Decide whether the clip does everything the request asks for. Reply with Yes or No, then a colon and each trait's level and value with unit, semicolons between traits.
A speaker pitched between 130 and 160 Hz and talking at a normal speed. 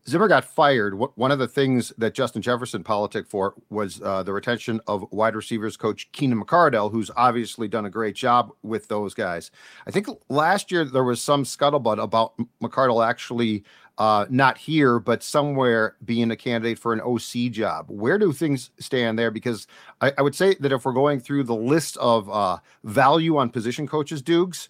No: low, 120 Hz; average, 190 wpm